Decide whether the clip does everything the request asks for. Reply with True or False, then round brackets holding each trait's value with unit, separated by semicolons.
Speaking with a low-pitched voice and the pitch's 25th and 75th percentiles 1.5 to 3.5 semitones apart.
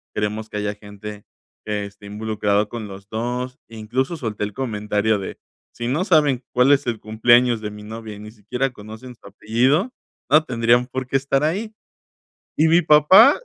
False (115 Hz; 4.1 semitones)